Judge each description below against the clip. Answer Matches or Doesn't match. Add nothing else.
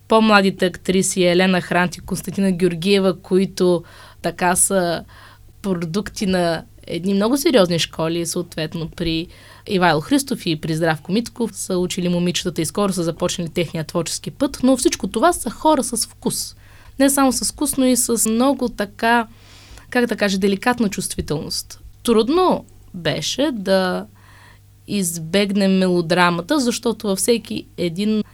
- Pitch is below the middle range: Doesn't match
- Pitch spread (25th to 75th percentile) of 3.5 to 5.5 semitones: Matches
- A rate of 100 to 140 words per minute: Matches